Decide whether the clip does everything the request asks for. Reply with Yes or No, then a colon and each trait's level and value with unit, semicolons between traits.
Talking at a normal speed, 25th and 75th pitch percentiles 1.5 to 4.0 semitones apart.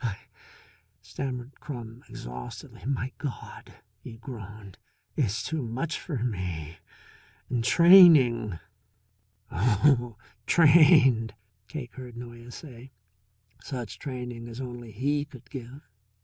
No: slow, 110 wpm; average, 3.5 semitones